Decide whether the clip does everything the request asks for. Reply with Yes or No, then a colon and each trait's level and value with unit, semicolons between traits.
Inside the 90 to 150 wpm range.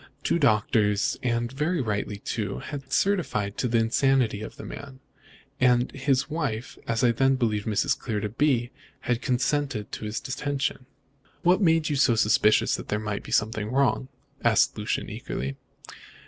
No: average, 160 wpm